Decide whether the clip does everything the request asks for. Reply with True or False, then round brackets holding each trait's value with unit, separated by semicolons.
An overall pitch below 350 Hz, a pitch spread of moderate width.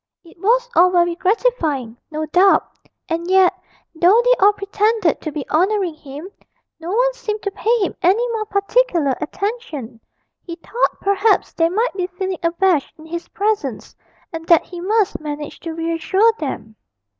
False (365 Hz; 4.4 semitones)